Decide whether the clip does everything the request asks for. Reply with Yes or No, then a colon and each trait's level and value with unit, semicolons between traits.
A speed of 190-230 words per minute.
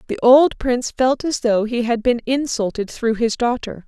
Yes: average, 200 wpm